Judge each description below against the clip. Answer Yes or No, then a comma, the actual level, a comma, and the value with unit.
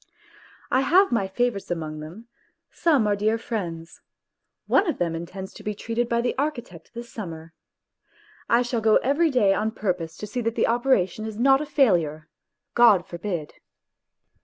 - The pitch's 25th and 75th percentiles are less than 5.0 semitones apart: No, wide, 5.6 semitones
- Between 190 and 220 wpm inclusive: No, average, 165 wpm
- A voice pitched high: Yes, high, 220 Hz